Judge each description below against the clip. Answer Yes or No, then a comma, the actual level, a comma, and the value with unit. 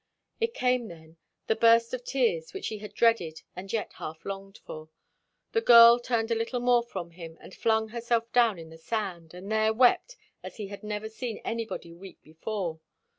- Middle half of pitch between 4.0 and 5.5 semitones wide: Yes, average, 4.8 semitones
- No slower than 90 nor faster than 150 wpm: No, average, 190 wpm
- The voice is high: Yes, high, 220 Hz